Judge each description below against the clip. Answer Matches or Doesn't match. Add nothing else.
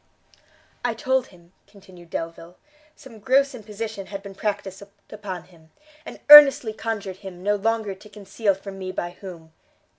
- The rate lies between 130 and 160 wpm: Matches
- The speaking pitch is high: Matches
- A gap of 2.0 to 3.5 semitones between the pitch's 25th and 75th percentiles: Matches